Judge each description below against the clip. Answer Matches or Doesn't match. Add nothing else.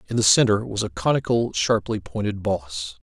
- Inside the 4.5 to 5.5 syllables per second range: Matches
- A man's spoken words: Matches